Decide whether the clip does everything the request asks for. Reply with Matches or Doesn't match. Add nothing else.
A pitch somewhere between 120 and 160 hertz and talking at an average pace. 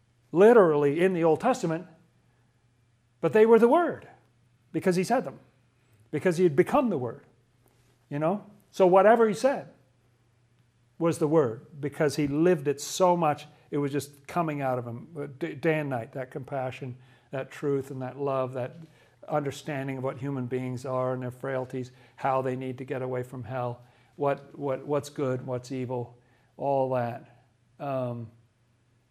Matches